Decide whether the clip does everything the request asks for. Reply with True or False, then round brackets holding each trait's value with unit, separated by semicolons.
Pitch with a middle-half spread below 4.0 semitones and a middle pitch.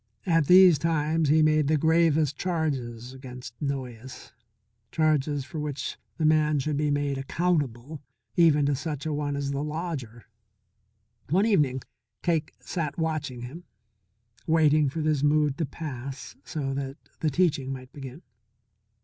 True (2.9 semitones; 150 Hz)